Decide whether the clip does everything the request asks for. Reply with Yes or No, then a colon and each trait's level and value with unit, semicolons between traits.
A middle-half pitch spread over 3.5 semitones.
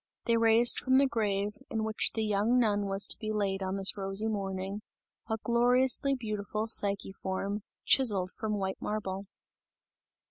No: narrow, 2.5 semitones